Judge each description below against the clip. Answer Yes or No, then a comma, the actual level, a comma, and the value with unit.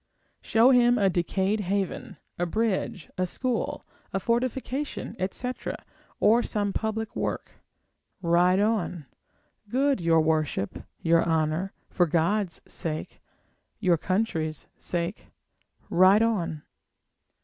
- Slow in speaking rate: Yes, slow, 105 wpm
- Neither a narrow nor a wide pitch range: Yes, average, 4.8 semitones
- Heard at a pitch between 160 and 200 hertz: Yes, high, 190 Hz